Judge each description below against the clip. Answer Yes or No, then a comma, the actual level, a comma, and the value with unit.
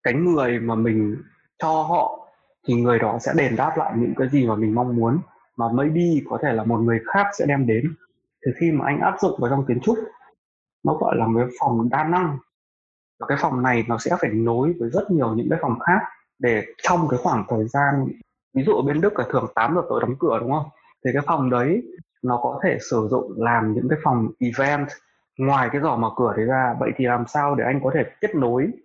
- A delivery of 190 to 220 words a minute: No, average, 240 wpm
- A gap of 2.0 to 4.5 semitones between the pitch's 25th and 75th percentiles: No, average, 4.9 semitones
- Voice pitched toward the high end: No, low, 130 Hz